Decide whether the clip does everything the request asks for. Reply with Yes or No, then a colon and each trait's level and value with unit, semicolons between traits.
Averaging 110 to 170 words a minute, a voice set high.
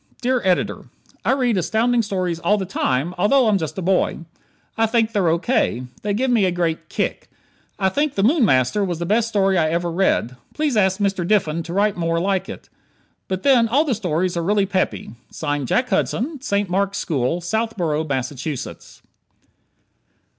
No: average, 185 wpm; high, 195 Hz